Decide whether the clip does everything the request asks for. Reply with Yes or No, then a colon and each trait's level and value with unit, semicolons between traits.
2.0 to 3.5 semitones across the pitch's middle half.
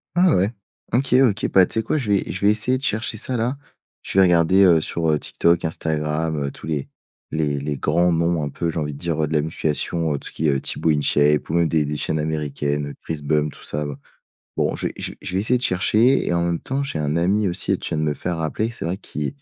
No: average, 4.4 semitones